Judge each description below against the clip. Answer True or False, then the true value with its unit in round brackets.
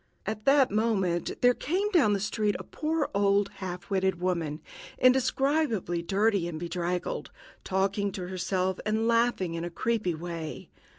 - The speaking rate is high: False (150 wpm)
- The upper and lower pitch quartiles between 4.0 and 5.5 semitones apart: True (4.5 semitones)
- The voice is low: False (195 Hz)